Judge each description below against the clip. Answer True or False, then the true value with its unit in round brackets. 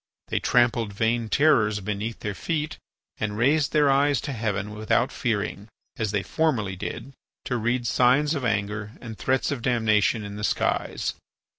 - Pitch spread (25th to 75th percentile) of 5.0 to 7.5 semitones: False (3.9 semitones)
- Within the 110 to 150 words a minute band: False (160 wpm)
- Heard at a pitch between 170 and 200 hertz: False (115 Hz)